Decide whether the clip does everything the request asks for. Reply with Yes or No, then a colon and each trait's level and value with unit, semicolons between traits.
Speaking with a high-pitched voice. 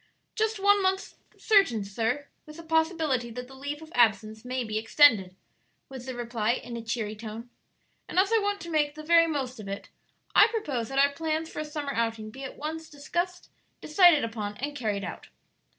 Yes: very high, 275 Hz